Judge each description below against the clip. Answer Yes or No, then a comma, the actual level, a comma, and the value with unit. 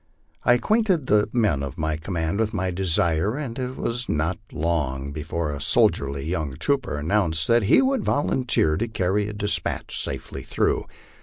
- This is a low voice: Yes, very low, 95 Hz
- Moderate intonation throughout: No, wide, 6.9 semitones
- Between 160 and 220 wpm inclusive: Yes, average, 165 wpm